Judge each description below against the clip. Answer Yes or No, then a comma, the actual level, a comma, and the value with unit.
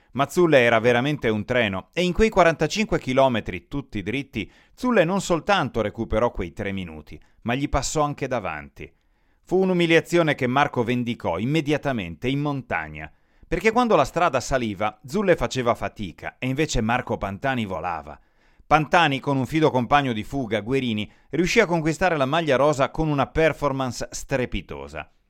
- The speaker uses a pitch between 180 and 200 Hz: No, low, 130 Hz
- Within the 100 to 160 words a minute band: Yes, average, 150 wpm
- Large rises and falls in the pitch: Yes, wide, 6.6 semitones